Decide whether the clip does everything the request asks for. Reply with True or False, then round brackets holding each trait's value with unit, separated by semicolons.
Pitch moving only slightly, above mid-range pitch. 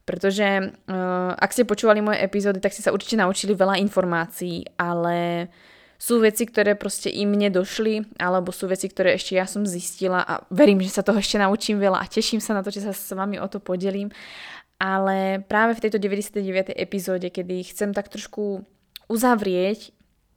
True (1.8 semitones; 195 Hz)